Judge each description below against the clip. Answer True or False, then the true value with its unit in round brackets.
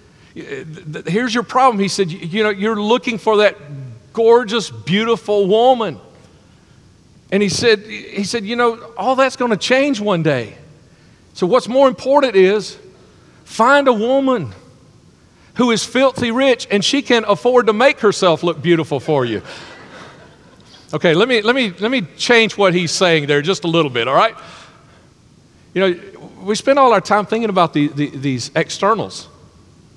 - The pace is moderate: True (165 wpm)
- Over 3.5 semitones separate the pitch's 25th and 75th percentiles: True (5.1 semitones)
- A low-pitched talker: False (215 Hz)